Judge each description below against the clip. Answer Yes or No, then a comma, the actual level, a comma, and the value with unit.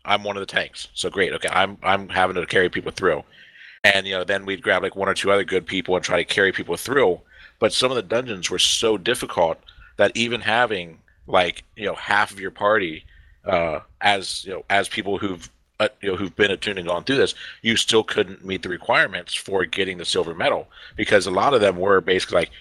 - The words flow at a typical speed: No, fast, 235 wpm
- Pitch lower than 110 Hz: Yes, low, 100 Hz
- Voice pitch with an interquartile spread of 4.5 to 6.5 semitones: No, average, 2.9 semitones